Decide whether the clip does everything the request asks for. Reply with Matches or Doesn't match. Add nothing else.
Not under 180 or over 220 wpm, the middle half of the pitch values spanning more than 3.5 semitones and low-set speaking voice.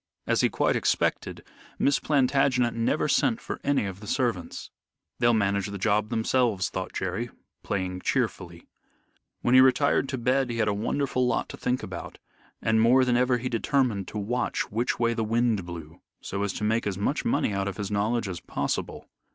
Matches